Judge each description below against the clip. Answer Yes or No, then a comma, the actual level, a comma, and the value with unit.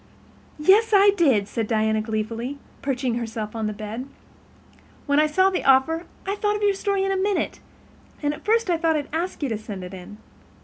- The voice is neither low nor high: No, very high, 285 Hz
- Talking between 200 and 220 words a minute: Yes, fast, 205 wpm